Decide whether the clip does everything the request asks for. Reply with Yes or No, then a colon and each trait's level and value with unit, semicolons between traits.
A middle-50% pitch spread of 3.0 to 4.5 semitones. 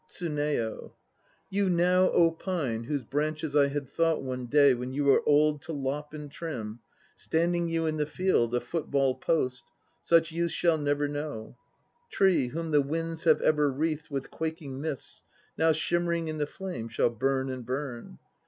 Yes: average, 3.4 semitones